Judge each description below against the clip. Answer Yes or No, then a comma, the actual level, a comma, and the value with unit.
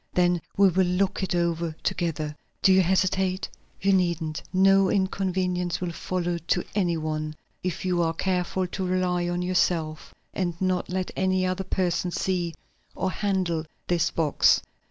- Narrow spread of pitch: Yes, narrow, 1.6 semitones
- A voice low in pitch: No, medium, 180 Hz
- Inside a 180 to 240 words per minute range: No, average, 155 wpm